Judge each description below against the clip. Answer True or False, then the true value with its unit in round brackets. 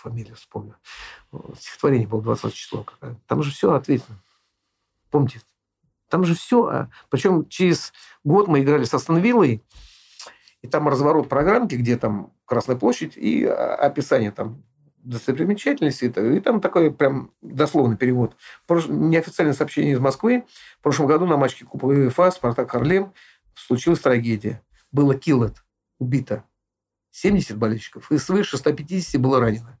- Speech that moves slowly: False (130 wpm)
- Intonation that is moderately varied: False (6.0 semitones)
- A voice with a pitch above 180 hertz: False (140 Hz)